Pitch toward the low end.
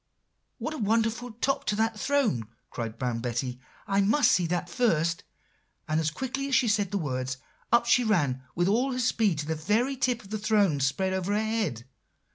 No: high, 205 Hz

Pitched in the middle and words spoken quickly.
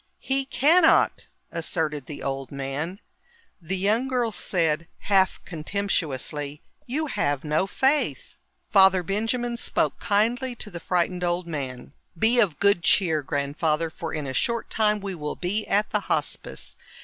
No: medium, 180 Hz; average, 145 wpm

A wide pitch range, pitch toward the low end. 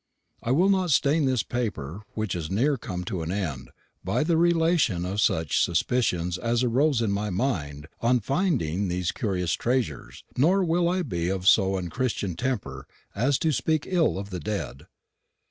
Yes: wide, 7.8 semitones; low, 110 Hz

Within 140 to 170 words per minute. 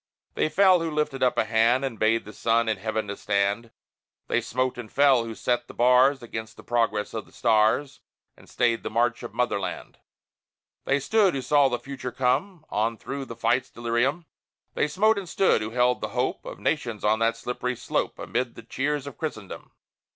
No: average, 195 wpm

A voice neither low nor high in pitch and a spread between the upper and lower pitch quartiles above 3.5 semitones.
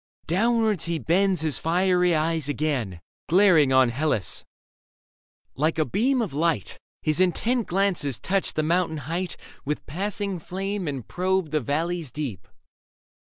Yes: medium, 165 Hz; average, 4.2 semitones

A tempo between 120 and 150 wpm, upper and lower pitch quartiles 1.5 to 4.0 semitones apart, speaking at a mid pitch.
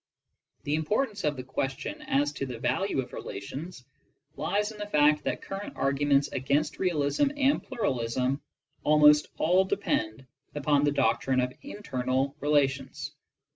No: average, 140 wpm; average, 5.1 semitones; medium, 145 Hz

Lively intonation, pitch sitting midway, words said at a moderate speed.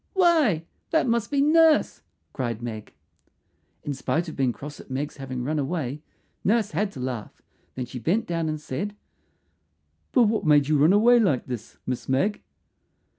Yes: wide, 8.7 semitones; medium, 155 Hz; average, 170 wpm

